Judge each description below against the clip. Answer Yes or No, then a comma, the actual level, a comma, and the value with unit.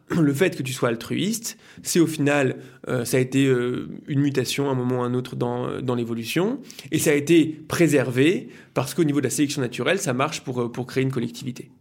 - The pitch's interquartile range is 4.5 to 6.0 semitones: No, average, 3.7 semitones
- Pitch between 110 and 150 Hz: Yes, low, 135 Hz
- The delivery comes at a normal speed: No, fast, 235 wpm